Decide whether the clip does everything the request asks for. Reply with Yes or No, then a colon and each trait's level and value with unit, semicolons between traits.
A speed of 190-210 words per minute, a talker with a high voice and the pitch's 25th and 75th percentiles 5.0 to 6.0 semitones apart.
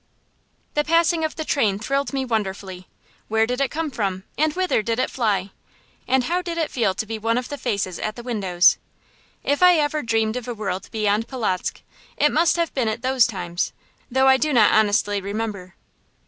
Yes: average, 200 wpm; high, 230 Hz; wide, 5.5 semitones